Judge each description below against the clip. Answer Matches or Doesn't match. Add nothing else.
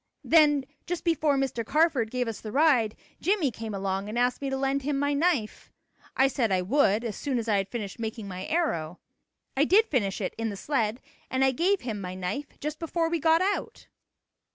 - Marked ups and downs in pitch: Matches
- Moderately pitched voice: Doesn't match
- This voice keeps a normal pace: Doesn't match